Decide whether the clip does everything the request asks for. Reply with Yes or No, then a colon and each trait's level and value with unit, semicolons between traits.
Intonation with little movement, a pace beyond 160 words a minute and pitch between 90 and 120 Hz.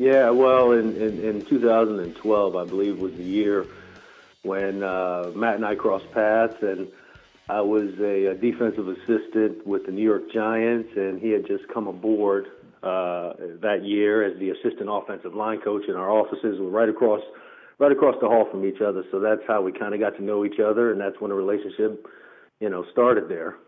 Yes: narrow, 2.3 semitones; average, 200 wpm; low, 105 Hz